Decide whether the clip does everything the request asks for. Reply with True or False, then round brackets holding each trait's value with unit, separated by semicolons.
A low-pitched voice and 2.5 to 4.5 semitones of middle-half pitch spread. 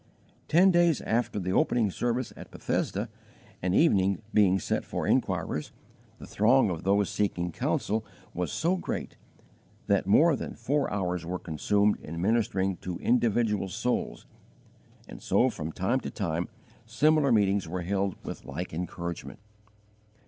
False (100 Hz; 5.0 semitones)